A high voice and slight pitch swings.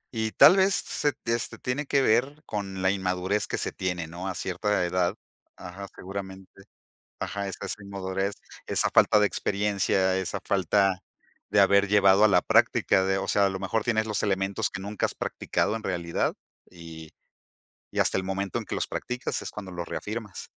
No: low, 100 Hz; narrow, 2.0 semitones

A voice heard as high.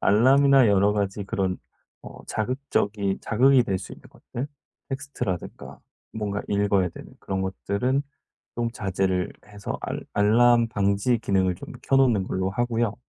No: low, 105 Hz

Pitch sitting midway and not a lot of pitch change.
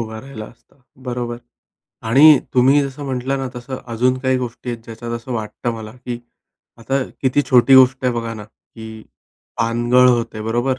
No: low, 125 Hz; narrow, 2.2 semitones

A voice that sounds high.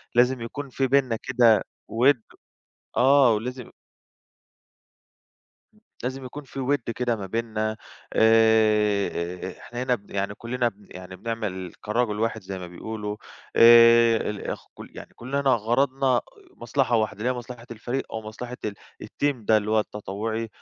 No: low, 115 Hz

